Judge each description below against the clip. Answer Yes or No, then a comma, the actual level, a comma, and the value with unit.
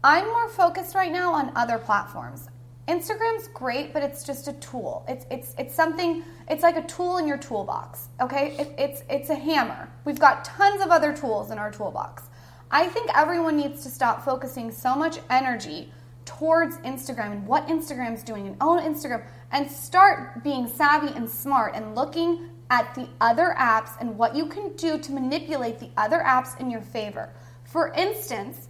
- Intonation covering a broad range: Yes, wide, 6.0 semitones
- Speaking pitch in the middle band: No, very high, 280 Hz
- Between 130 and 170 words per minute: No, average, 180 wpm